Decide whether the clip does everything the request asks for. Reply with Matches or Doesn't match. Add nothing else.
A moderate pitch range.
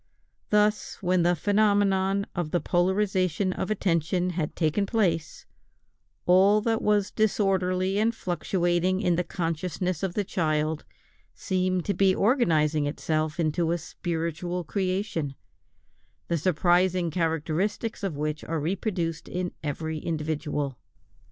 Matches